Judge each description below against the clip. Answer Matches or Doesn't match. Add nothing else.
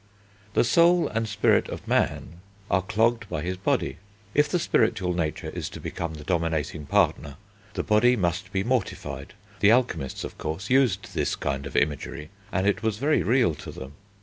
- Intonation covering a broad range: Matches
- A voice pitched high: Doesn't match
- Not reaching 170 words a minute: Doesn't match